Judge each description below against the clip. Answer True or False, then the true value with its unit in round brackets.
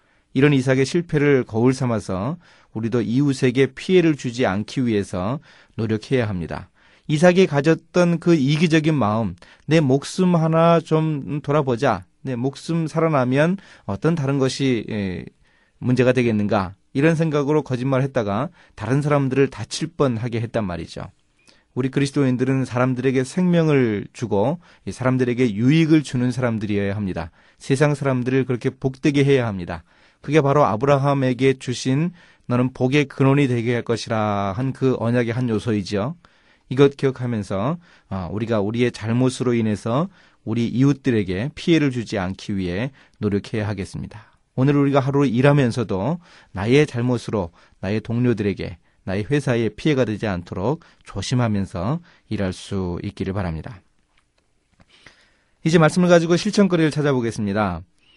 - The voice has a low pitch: True (130 Hz)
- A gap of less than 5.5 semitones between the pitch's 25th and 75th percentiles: True (5.1 semitones)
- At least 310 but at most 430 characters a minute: True (330 characters per minute)